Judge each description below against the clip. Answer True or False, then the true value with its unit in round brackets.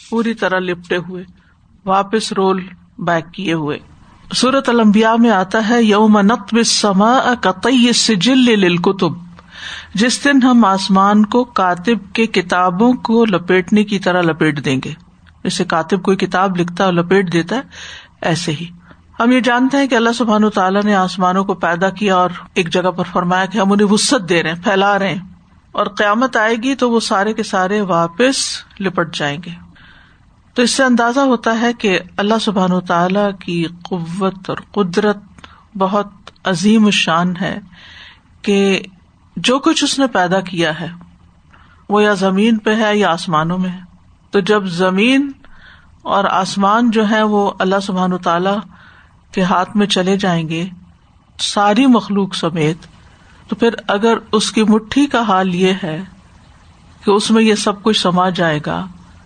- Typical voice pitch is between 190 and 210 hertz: True (195 Hz)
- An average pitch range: True (3.6 semitones)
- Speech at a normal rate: True (165 wpm)